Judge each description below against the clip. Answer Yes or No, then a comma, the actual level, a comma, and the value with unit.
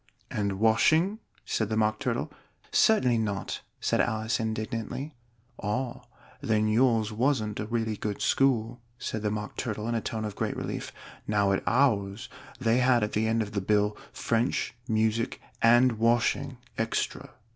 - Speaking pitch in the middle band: No, low, 110 Hz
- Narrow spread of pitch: Yes, narrow, 2.1 semitones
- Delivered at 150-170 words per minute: Yes, average, 155 wpm